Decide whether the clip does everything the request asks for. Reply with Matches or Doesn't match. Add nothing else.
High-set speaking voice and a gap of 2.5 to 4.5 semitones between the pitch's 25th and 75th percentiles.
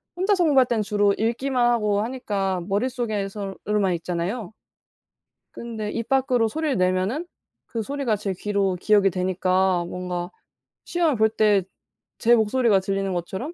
Matches